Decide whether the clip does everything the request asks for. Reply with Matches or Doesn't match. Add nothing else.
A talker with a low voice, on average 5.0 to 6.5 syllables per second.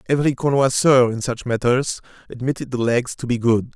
Matches